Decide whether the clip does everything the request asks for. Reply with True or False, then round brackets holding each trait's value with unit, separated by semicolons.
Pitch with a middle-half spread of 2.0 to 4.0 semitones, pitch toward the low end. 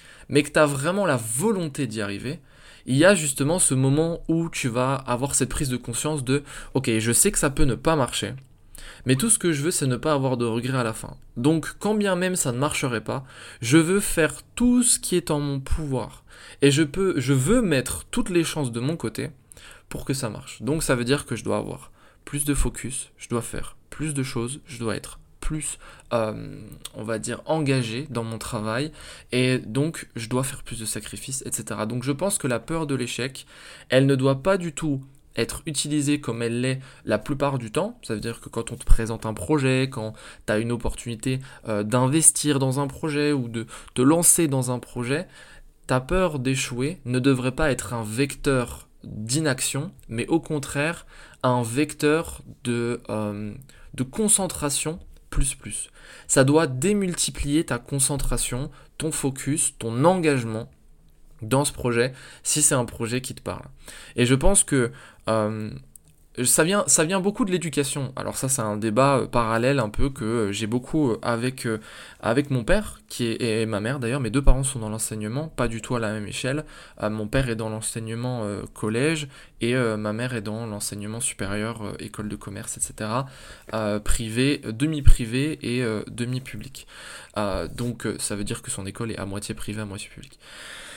False (4.5 semitones; 130 Hz)